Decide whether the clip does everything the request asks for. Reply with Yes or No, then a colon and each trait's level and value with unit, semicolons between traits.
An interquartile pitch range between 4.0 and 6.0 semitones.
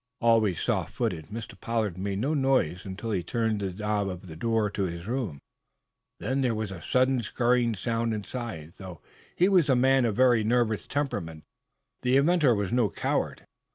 Yes: average, 4.5 semitones